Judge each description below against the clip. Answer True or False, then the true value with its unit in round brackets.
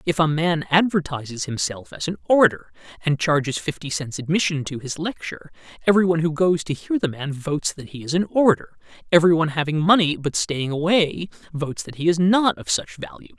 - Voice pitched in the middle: True (155 Hz)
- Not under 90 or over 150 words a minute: False (195 wpm)